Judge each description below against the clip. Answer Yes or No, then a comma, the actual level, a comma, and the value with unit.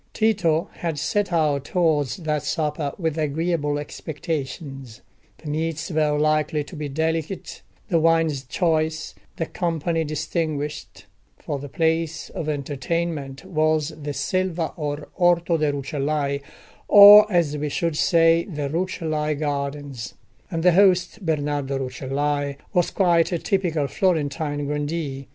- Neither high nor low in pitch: Yes, medium, 155 Hz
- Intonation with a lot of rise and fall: No, narrow, 2.4 semitones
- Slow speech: Yes, slow, 130 wpm